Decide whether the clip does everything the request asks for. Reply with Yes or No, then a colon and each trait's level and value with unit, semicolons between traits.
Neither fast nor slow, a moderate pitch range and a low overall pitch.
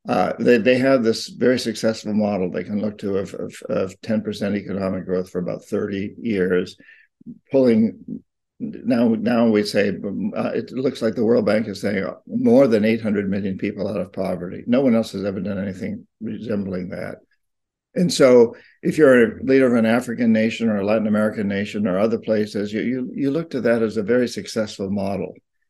Yes: average, 190 wpm; average, 3.5 semitones; low, 110 Hz